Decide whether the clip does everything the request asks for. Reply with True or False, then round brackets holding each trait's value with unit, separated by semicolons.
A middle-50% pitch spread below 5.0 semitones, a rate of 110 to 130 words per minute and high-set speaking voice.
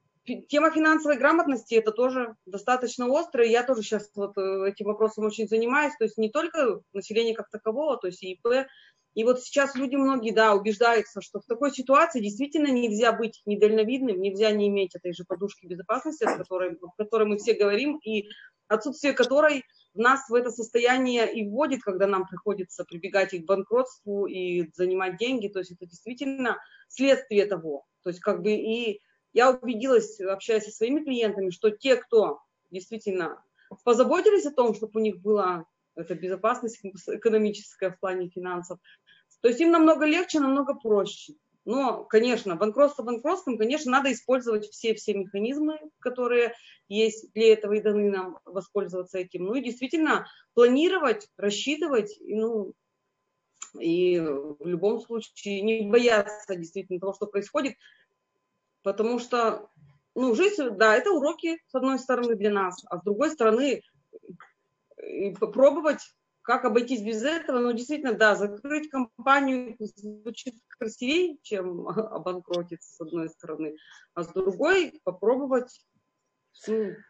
False (4.6 semitones; 145 wpm; 220 Hz)